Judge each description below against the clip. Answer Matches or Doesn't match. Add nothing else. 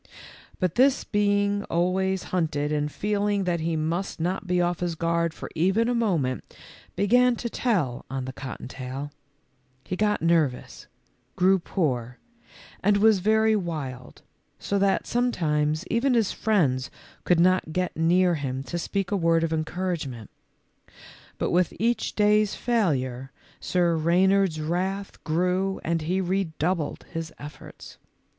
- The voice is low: Doesn't match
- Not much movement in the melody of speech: Doesn't match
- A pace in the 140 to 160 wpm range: Matches